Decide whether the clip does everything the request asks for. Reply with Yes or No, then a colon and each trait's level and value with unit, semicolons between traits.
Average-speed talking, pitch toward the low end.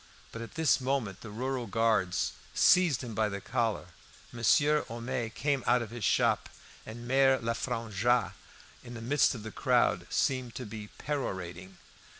Yes: average, 155 wpm; low, 120 Hz